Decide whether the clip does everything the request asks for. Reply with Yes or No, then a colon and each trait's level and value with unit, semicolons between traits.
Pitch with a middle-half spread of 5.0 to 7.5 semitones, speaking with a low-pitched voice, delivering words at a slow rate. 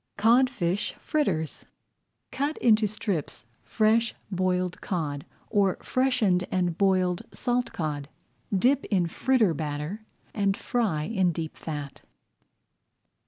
No: wide, 5.5 semitones; high, 190 Hz; slow, 105 wpm